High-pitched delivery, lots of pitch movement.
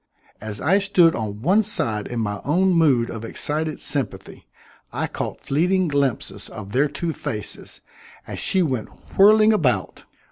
No: medium, 145 Hz; wide, 8.4 semitones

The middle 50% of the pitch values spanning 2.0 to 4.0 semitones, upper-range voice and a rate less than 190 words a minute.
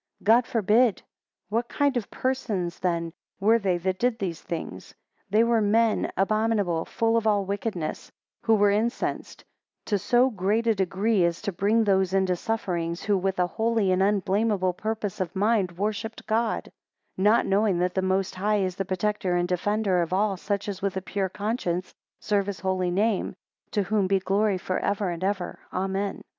Yes: average, 2.8 semitones; high, 200 Hz; average, 180 wpm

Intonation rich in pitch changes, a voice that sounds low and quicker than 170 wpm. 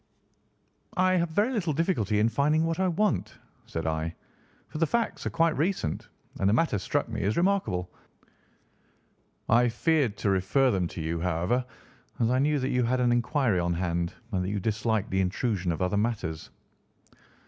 Yes: wide, 9.0 semitones; low, 115 Hz; average, 180 wpm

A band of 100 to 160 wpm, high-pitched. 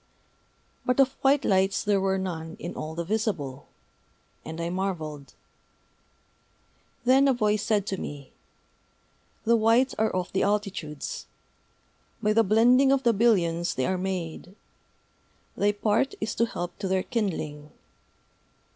Yes: average, 140 wpm; high, 195 Hz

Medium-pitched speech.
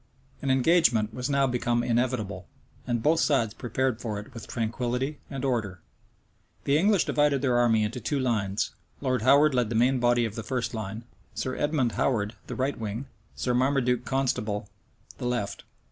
No: low, 125 Hz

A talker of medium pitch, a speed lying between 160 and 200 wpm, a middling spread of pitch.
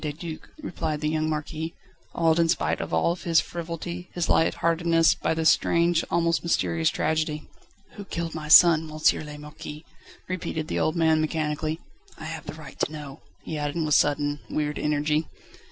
No: medium, 160 Hz; average, 175 wpm; narrow, 1.7 semitones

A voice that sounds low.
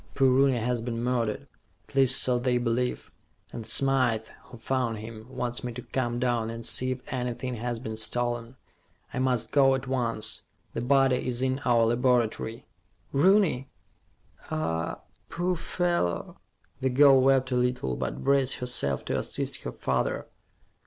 Yes: low, 125 Hz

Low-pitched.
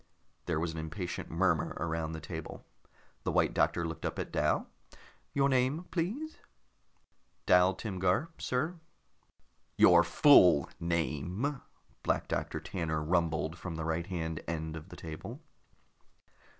Yes: very low, 85 Hz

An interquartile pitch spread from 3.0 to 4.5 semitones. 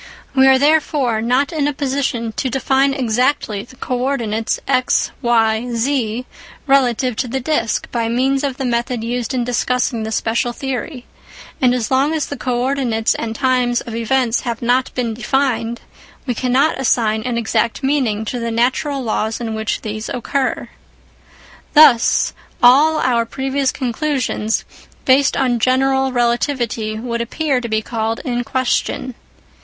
No: narrow, 2.6 semitones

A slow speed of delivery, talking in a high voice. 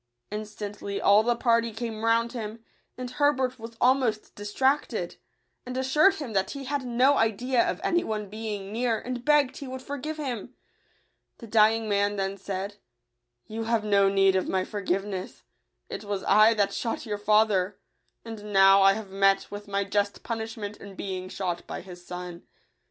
No: average, 180 wpm; high, 215 Hz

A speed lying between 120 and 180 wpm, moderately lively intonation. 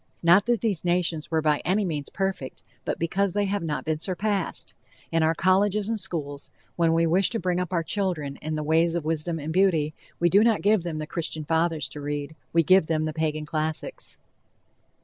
No: fast, 205 wpm; average, 3.4 semitones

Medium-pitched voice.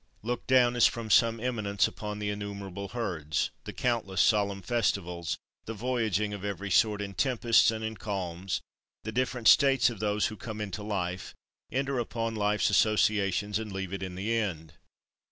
No: low, 105 Hz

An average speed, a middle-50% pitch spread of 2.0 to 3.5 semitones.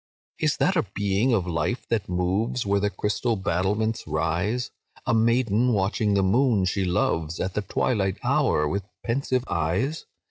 No: average, 155 wpm; average, 4.1 semitones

